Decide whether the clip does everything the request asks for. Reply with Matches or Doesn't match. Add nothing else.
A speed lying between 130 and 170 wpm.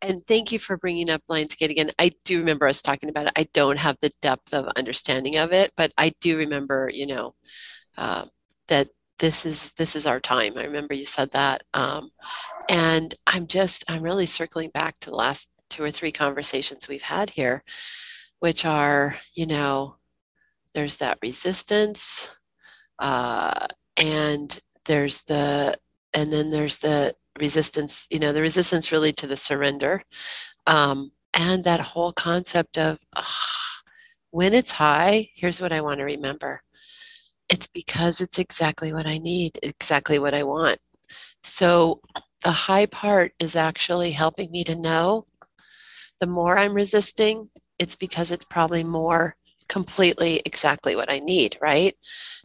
Matches